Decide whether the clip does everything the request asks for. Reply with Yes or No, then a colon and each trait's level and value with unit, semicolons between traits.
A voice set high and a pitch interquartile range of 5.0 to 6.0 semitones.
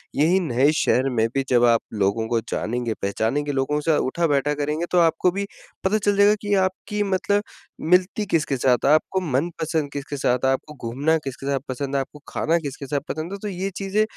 No: medium, 150 Hz; wide, 5.4 semitones